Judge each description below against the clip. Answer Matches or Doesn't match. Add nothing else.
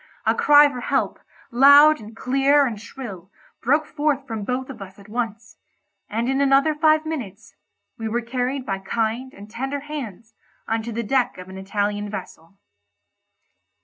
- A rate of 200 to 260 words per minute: Doesn't match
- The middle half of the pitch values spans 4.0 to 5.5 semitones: Matches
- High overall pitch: Matches